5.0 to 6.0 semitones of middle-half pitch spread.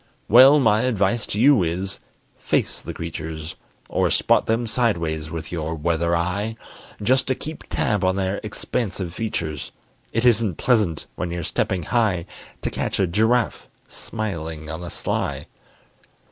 Yes: average, 5.3 semitones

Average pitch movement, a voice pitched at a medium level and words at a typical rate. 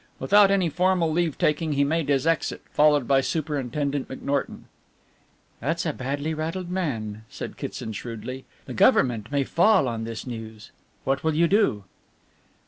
Yes: average, 4.4 semitones; medium, 145 Hz; average, 150 wpm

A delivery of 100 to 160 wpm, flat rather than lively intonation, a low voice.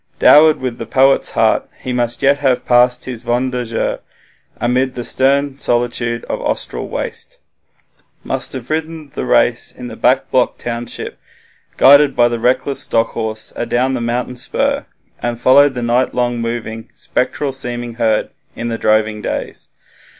Yes: average, 155 wpm; narrow, 2.0 semitones; low, 125 Hz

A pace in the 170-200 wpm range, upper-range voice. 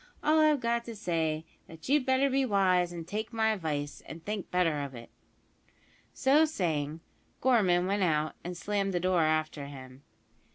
No: average, 175 wpm; medium, 180 Hz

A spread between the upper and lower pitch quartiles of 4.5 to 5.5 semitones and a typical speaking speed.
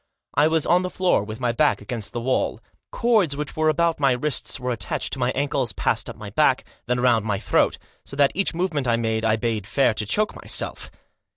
No: average, 5.2 semitones; fast, 220 wpm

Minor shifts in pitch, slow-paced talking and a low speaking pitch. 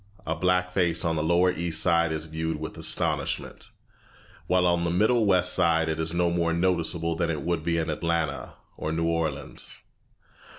No: narrow, 1.5 semitones; average, 180 wpm; very low, 85 Hz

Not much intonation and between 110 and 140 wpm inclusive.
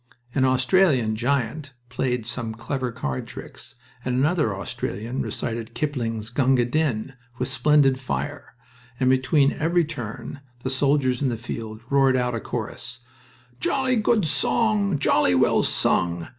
No: average, 3.9 semitones; slow, 135 wpm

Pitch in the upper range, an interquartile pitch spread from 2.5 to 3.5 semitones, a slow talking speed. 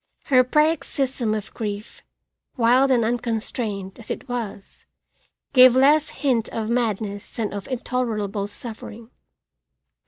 Yes: high, 235 Hz; average, 3.2 semitones; slow, 115 wpm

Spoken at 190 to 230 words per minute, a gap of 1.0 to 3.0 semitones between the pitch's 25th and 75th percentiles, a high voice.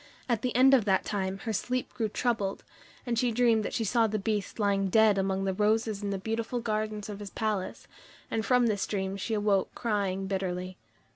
Yes: fast, 205 wpm; narrow, 2.6 semitones; high, 210 Hz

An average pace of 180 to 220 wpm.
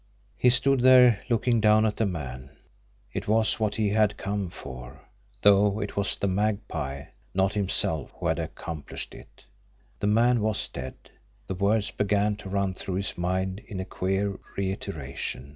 No: average, 160 wpm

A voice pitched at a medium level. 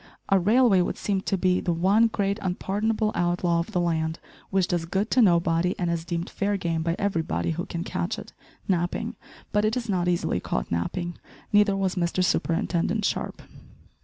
Yes: medium, 180 Hz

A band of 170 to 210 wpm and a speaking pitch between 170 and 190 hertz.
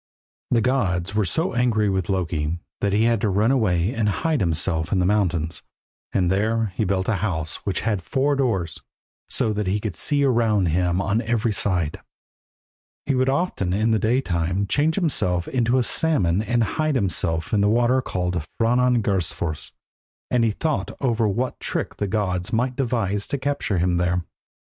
No: average, 175 wpm; low, 105 Hz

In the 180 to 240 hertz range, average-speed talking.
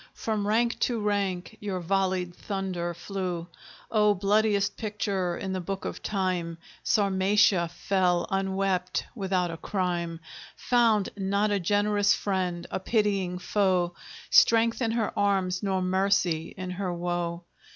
No: high, 190 Hz; slow, 130 wpm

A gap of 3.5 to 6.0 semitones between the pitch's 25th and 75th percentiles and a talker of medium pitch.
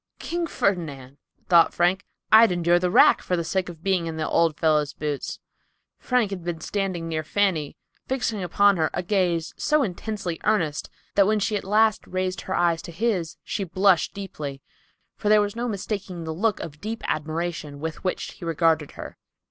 Yes: average, 3.9 semitones; medium, 175 Hz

